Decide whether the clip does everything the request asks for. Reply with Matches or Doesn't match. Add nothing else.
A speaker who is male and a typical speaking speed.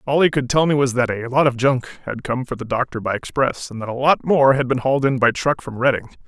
Doesn't match